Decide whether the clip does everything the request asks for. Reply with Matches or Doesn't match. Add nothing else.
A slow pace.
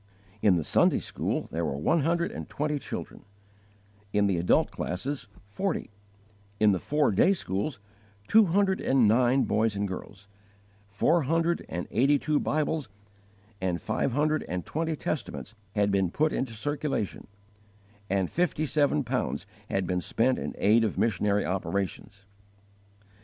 Doesn't match